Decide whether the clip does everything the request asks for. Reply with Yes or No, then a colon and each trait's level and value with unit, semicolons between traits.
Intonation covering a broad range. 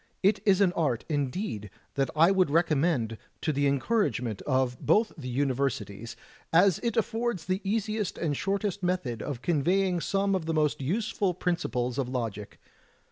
Yes: wide, 6.9 semitones